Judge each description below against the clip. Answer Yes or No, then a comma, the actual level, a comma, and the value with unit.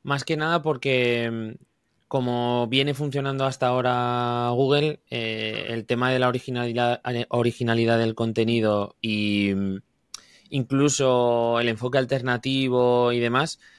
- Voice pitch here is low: Yes, low, 120 Hz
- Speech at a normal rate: No, slow, 115 wpm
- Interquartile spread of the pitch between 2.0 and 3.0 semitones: Yes, narrow, 2.5 semitones